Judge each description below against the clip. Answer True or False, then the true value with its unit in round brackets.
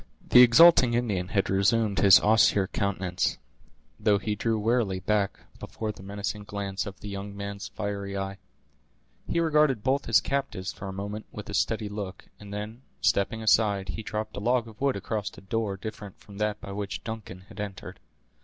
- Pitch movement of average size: False (2.2 semitones)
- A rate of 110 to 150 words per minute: False (180 wpm)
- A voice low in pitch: True (105 Hz)